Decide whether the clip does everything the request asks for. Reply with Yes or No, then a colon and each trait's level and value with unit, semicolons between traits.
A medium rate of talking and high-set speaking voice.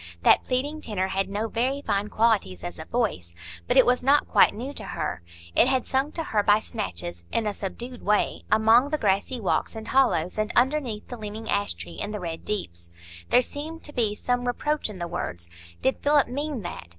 No: fast, 210 wpm; high, 220 Hz